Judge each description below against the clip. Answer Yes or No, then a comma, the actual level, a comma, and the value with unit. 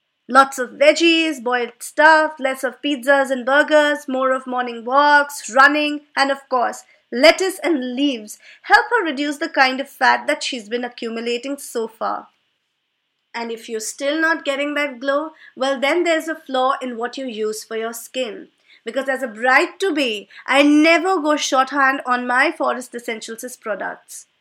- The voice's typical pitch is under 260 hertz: No, very high, 270 Hz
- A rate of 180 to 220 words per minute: No, average, 170 wpm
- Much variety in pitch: No, average, 3.2 semitones